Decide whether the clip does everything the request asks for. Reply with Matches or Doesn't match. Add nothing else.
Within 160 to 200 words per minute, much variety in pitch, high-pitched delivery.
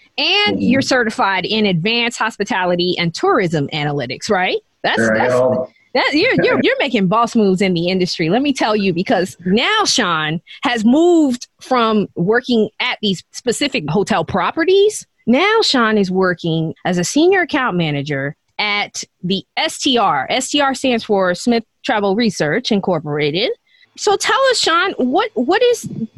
Doesn't match